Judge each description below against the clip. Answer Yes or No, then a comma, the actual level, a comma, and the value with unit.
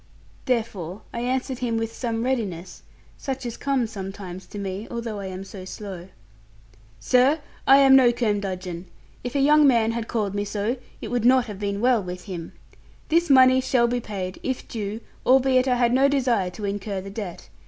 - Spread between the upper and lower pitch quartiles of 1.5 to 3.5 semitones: No, average, 4.4 semitones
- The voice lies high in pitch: Yes, high, 225 Hz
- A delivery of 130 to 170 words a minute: No, average, 185 wpm